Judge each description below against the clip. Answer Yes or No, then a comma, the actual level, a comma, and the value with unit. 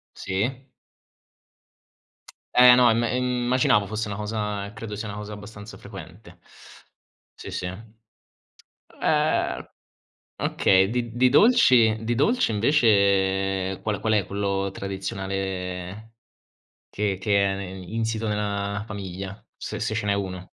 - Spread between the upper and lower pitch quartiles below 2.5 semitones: No, average, 2.8 semitones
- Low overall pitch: Yes, low, 105 Hz